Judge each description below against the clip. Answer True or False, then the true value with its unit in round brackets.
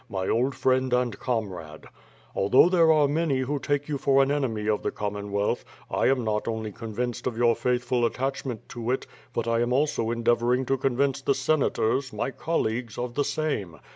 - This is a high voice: False (125 Hz)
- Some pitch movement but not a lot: True (3.4 semitones)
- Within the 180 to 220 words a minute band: True (185 wpm)